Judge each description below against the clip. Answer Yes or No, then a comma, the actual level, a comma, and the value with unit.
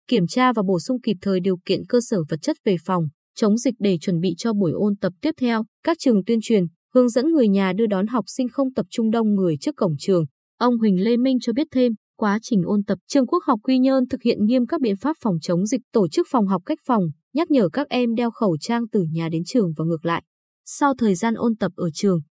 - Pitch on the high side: Yes, high, 220 Hz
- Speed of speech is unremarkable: No, fast, 265 wpm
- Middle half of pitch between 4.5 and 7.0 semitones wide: Yes, average, 5.0 semitones